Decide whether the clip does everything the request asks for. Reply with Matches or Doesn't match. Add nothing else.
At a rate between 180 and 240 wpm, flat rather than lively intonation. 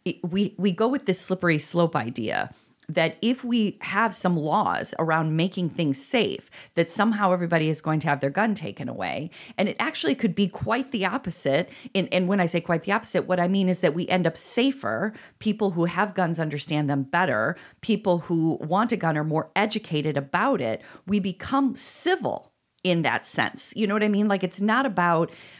Doesn't match